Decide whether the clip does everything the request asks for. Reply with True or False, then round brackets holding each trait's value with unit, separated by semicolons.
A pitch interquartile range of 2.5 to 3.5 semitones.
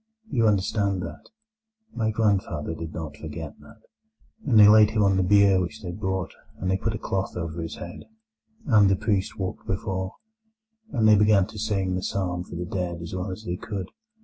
True (3.0 semitones)